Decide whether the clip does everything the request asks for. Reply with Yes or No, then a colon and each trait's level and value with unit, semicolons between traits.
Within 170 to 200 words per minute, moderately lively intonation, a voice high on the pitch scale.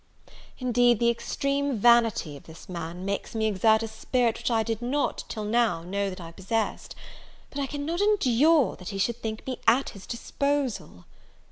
Yes: average, 175 wpm; average, 4.5 semitones; high, 230 Hz